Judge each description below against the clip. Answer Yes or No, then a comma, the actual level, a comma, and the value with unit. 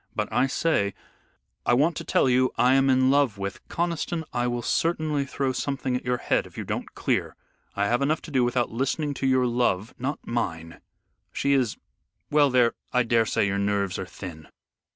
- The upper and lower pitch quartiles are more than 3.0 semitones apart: Yes, average, 3.5 semitones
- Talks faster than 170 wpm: Yes, average, 200 wpm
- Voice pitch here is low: Yes, low, 125 Hz